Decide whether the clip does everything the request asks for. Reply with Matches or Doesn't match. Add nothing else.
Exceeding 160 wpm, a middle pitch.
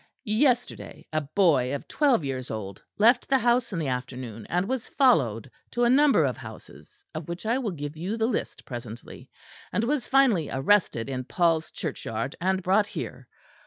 Matches